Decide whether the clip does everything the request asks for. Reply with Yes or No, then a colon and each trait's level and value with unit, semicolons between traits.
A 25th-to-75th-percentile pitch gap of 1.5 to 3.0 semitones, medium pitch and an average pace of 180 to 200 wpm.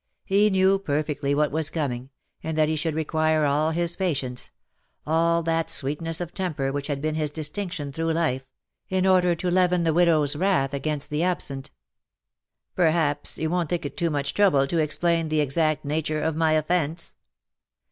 Yes: average, 2.7 semitones; medium, 160 Hz; average, 185 wpm